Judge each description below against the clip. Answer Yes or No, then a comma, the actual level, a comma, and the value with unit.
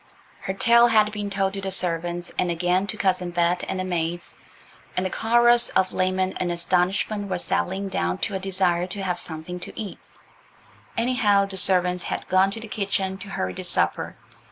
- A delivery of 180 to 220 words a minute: Yes, average, 190 wpm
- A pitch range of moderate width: No, narrow, 2.1 semitones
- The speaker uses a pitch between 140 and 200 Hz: Yes, high, 190 Hz